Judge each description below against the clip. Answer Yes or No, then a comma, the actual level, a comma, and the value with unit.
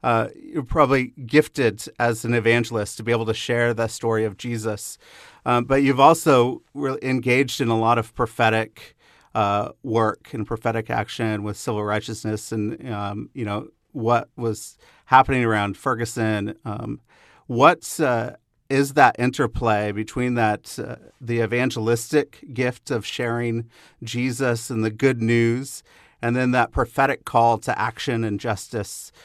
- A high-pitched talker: No, low, 115 Hz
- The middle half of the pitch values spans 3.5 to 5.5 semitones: No, narrow, 2.5 semitones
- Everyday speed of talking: Yes, average, 150 wpm